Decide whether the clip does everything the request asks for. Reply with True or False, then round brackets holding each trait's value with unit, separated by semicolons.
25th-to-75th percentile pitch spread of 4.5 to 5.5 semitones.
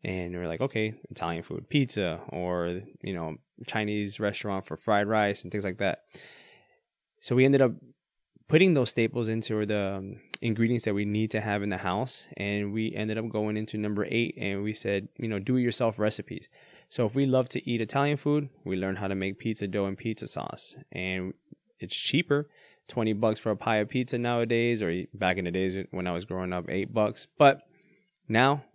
False (3.5 semitones)